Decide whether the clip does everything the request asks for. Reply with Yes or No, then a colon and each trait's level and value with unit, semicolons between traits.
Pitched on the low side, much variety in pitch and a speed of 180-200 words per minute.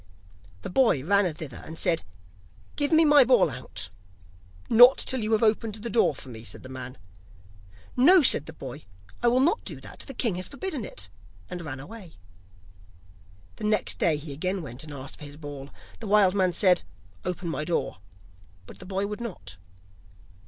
No: medium, 185 Hz; wide, 7.9 semitones; average, 185 wpm